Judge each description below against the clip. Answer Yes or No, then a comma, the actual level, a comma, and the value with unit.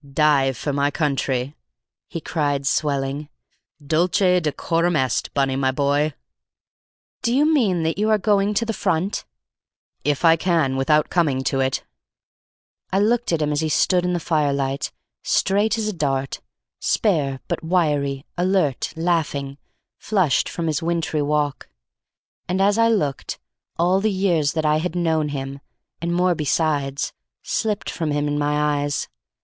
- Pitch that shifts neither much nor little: Yes, average, 4.1 semitones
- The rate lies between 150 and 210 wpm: Yes, average, 155 wpm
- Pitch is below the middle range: No, medium, 155 Hz